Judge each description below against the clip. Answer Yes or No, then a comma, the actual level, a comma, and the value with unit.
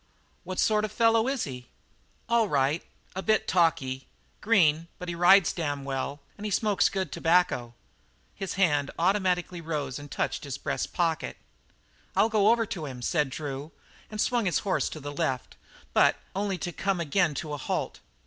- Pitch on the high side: No, medium, 170 Hz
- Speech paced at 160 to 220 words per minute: Yes, average, 175 wpm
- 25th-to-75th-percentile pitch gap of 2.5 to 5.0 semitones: No, wide, 5.5 semitones